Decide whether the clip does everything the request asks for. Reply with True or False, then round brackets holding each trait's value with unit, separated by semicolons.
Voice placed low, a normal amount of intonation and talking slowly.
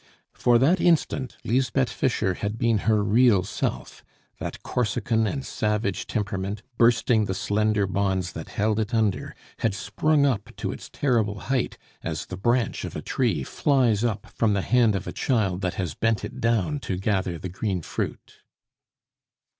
False (110 Hz; 3.5 semitones; 165 wpm)